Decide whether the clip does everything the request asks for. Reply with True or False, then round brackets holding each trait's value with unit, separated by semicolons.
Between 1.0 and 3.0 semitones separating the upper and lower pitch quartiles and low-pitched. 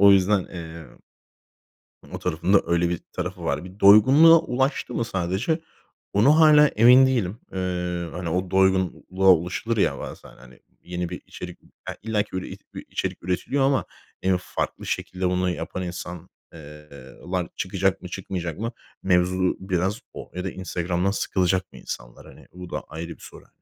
True (2.6 semitones; 95 Hz)